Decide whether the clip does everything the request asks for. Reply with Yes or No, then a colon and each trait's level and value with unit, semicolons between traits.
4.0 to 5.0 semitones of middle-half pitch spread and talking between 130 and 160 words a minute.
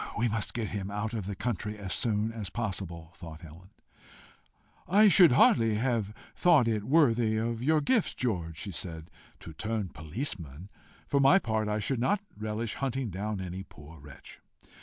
No: average, 4.3 semitones; average, 175 wpm